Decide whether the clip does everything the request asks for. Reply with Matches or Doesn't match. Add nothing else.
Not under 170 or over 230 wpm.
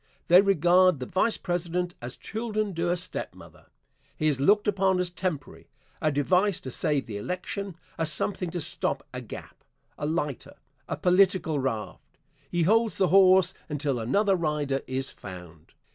Doesn't match